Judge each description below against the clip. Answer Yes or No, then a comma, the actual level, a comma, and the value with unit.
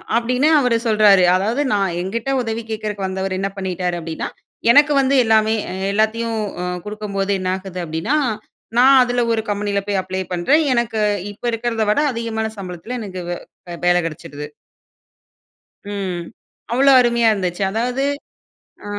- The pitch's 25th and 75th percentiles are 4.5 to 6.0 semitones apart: No, average, 3.7 semitones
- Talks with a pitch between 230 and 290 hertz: No, high, 215 Hz